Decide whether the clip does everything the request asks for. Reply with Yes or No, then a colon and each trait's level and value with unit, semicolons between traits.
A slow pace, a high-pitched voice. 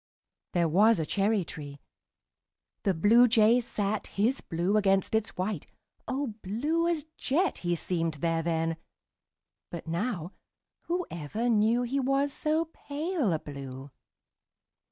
Yes: slow, 125 wpm; high, 210 Hz